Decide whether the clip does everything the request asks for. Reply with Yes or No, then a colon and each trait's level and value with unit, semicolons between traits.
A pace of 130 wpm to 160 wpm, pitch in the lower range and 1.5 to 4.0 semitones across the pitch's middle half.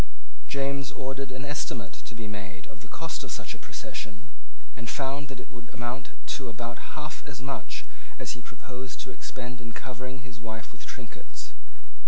No: average, 180 wpm; low, 125 Hz; average, 2.9 semitones